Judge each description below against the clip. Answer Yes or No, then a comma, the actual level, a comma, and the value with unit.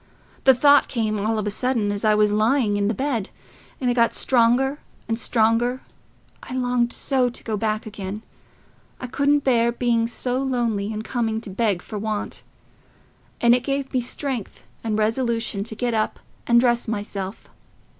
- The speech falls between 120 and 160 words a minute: No, average, 175 wpm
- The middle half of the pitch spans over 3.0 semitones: No, average, 2.7 semitones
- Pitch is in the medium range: No, high, 230 Hz